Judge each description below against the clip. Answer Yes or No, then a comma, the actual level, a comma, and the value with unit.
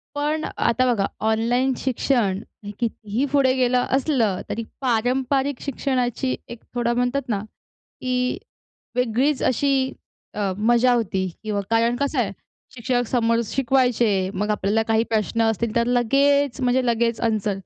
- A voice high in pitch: Yes, high, 240 Hz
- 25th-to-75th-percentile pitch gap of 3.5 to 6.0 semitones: No, average, 2.8 semitones